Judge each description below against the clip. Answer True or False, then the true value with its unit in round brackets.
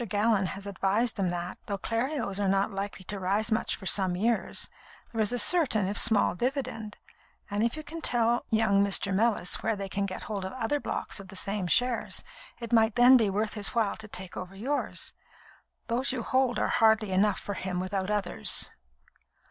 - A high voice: True (210 Hz)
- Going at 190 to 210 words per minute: True (195 wpm)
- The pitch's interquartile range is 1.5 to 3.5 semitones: True (3.1 semitones)